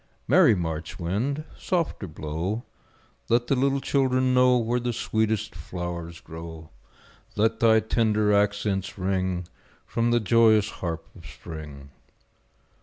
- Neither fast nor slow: No, slow, 120 wpm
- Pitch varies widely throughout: Yes, wide, 5.7 semitones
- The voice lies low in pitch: Yes, low, 105 Hz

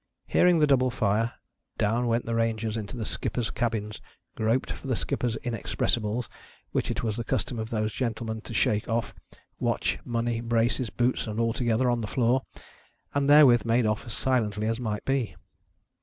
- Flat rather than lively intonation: Yes, narrow, 1.9 semitones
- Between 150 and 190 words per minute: Yes, average, 175 wpm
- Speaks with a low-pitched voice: Yes, low, 115 Hz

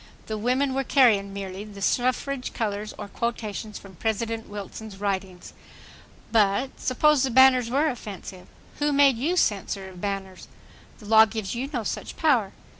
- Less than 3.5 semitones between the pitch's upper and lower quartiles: No, average, 4.4 semitones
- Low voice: No, high, 220 Hz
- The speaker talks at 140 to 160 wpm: Yes, average, 155 wpm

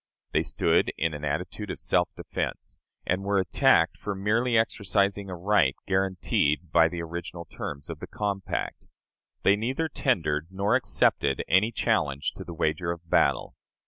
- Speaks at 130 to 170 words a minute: Yes, average, 155 wpm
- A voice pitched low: Yes, very low, 95 Hz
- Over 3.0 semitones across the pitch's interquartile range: Yes, average, 3.8 semitones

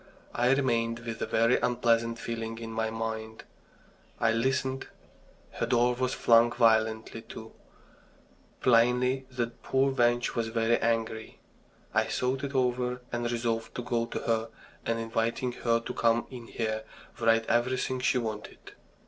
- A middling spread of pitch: No, narrow, 1.6 semitones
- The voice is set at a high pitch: No, low, 115 Hz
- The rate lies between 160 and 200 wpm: No, average, 145 wpm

